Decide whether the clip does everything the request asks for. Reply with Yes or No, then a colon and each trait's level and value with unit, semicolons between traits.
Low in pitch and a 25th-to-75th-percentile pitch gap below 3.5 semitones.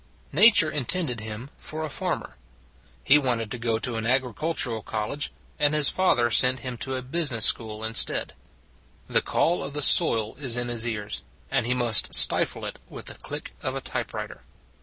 No: low, 125 Hz; average, 4.2 semitones